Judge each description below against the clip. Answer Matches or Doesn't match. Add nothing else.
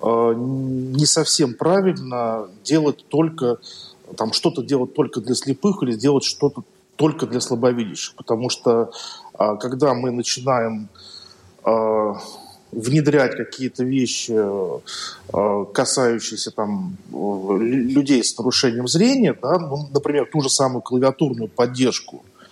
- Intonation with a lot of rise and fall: Doesn't match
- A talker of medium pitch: Doesn't match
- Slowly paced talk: Matches